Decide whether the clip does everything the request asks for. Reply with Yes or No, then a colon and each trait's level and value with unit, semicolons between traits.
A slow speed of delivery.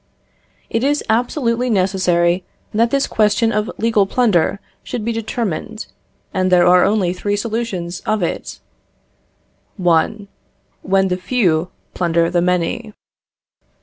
Yes: slow, 120 wpm